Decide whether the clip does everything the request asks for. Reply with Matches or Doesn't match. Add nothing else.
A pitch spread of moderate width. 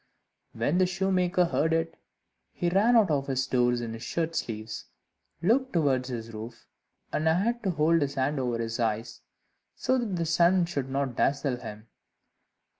Doesn't match